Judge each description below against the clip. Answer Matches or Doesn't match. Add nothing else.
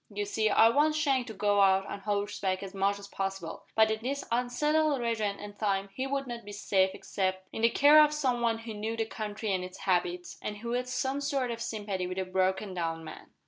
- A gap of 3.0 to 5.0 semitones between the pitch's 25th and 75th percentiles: Matches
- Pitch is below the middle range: Doesn't match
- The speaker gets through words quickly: Matches